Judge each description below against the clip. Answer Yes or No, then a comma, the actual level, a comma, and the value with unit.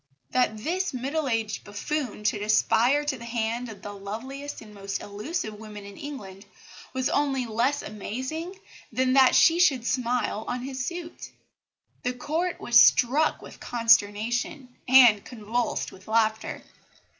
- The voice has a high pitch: Yes, high, 245 Hz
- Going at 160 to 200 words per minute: No, average, 145 wpm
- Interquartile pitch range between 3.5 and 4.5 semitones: Yes, average, 4.2 semitones